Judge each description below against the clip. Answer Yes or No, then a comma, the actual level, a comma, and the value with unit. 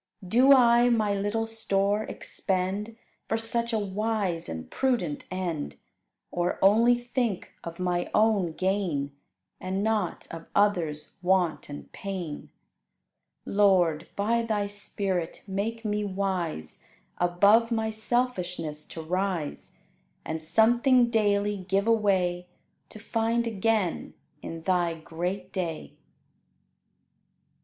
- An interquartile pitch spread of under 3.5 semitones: No, average, 4.1 semitones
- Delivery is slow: Yes, slow, 110 wpm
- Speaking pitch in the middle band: No, high, 200 Hz